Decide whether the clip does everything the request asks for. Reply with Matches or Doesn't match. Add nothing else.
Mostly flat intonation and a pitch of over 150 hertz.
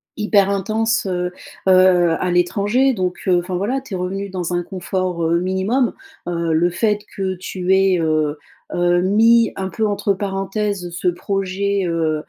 Matches